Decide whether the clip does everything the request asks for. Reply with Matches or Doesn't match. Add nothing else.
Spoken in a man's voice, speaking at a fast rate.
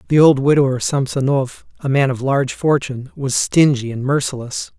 Doesn't match